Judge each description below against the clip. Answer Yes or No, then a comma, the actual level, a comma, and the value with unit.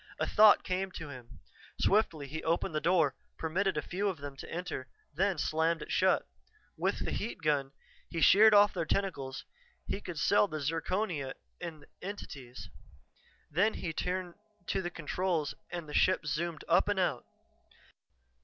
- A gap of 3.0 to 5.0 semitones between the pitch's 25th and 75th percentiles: Yes, average, 3.9 semitones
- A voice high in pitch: No, medium, 165 Hz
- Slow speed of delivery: No, average, 165 wpm